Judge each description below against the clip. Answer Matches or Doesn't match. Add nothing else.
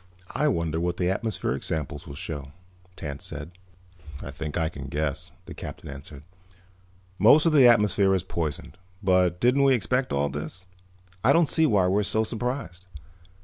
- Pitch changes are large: Matches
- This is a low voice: Matches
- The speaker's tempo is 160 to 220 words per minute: Matches